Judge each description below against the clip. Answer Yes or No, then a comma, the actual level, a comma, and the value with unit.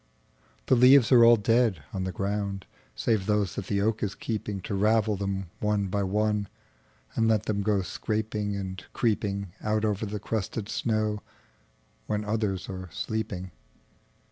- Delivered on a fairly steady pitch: Yes, narrow, 2.1 semitones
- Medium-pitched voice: No, low, 105 Hz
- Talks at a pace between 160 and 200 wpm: No, slow, 135 wpm